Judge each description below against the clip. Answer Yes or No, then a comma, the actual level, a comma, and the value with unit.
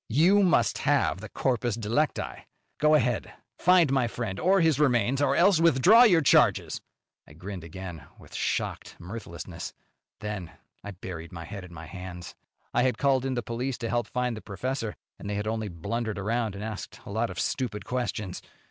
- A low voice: Yes, low, 115 Hz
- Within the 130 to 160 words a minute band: No, average, 185 wpm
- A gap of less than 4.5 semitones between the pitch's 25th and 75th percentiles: No, wide, 5.4 semitones